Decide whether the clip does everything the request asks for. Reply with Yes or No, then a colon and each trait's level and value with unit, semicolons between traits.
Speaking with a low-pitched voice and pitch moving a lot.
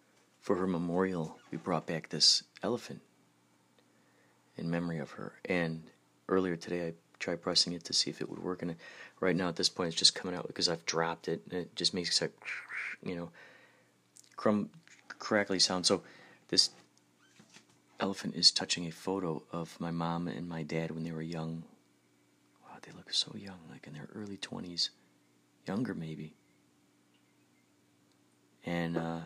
Yes: very low, 80 Hz; wide, 6.3 semitones